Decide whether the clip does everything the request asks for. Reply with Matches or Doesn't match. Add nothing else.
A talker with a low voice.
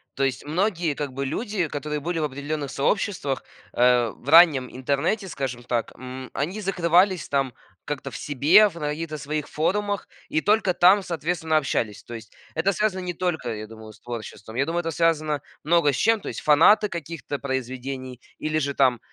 Doesn't match